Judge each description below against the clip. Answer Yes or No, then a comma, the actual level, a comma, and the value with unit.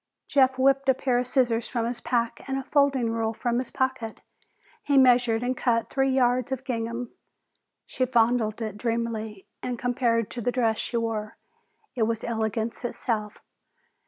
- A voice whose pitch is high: Yes, high, 240 Hz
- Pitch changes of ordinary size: No, narrow, 2.2 semitones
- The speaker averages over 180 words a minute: No, average, 165 wpm